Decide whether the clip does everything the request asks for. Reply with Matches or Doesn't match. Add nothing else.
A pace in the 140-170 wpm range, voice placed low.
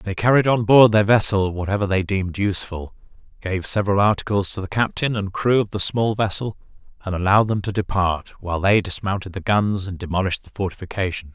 Doesn't match